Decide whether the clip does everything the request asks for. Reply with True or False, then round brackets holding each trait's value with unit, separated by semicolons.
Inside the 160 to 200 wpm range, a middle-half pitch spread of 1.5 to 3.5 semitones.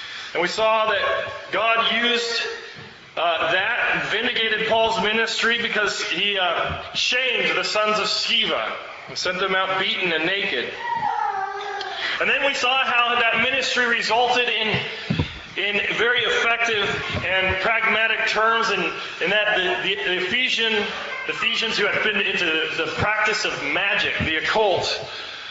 False (145 wpm; 2.8 semitones)